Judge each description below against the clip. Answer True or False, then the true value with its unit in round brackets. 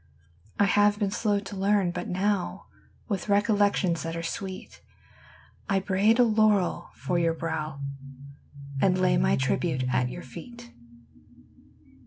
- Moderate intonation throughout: True (3.6 semitones)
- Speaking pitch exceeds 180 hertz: True (190 Hz)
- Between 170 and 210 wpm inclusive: False (140 wpm)